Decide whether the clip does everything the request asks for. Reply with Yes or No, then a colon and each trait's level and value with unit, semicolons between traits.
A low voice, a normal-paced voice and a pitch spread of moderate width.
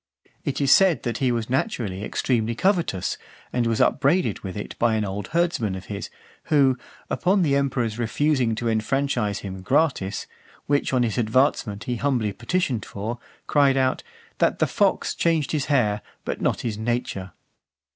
Yes: low, 120 Hz; average, 165 wpm; average, 4.8 semitones